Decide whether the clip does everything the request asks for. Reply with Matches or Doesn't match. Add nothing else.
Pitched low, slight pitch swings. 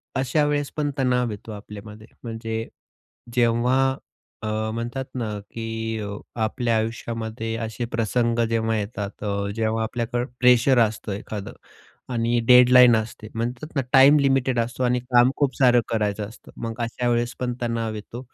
Matches